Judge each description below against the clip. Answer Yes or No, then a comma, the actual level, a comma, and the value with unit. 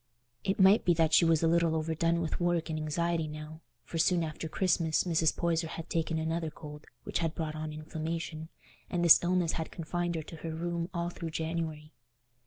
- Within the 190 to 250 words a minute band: Yes, average, 195 wpm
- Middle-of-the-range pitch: Yes, medium, 165 Hz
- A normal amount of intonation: No, narrow, 1.4 semitones